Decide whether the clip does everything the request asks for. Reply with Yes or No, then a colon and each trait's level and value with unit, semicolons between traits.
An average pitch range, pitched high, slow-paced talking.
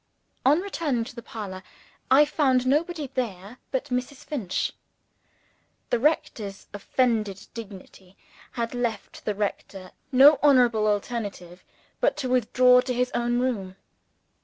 Yes: average, 4.2 semitones; high, 240 Hz; slow, 125 wpm